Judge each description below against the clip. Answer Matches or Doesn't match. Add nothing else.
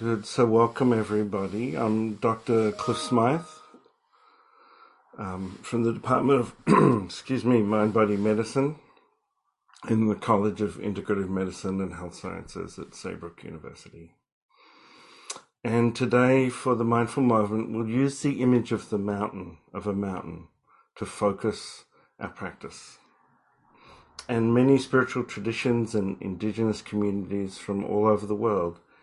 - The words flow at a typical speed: Doesn't match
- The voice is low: Matches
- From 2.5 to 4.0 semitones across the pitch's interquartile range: Matches